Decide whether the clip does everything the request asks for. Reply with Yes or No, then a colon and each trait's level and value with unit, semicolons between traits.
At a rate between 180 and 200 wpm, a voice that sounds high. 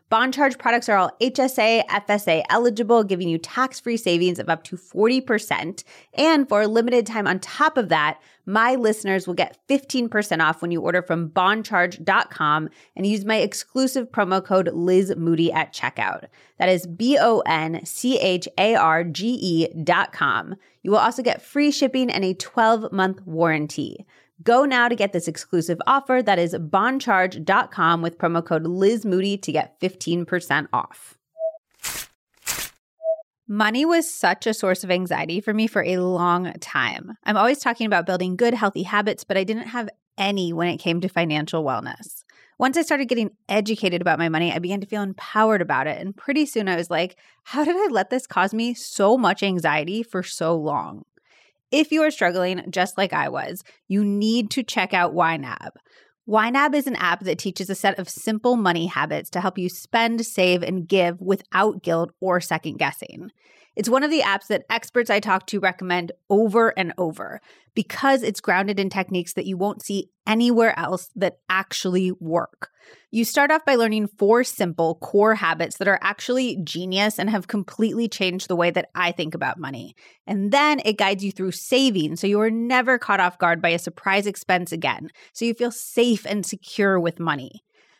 Yes: average, 185 wpm; high, 195 Hz